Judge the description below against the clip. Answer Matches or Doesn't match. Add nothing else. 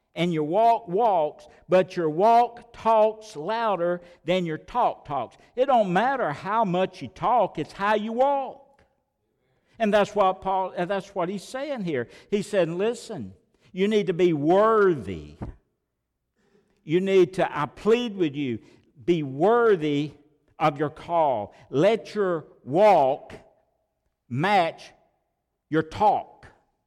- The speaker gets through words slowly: Matches